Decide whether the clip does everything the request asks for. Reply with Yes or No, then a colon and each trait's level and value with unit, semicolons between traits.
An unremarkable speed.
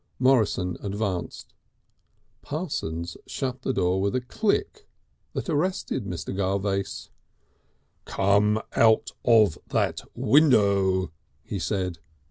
No: slow, 95 wpm